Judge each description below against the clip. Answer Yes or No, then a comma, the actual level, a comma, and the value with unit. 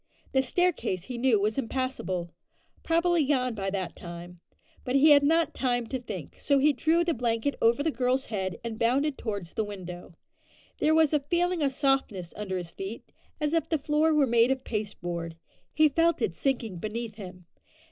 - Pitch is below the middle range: No, very high, 250 Hz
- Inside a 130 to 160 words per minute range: No, average, 185 wpm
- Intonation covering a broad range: Yes, wide, 6.7 semitones